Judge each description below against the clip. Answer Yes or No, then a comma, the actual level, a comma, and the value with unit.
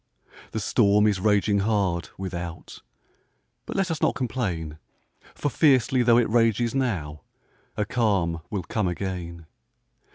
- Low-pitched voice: Yes, low, 105 Hz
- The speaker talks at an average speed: No, slow, 130 wpm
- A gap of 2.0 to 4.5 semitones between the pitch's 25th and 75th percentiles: No, average, 5.2 semitones